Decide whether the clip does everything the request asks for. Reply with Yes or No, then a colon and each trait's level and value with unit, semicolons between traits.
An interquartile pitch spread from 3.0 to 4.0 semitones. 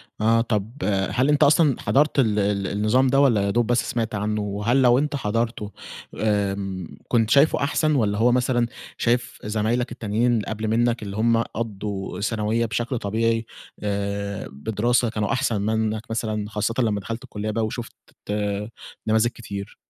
No: narrow, 2.5 semitones